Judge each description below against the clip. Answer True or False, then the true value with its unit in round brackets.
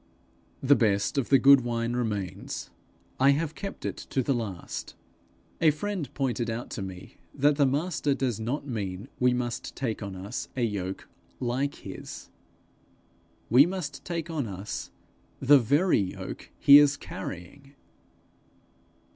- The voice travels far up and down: False (4.5 semitones)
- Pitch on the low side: True (130 Hz)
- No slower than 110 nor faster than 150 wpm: True (145 wpm)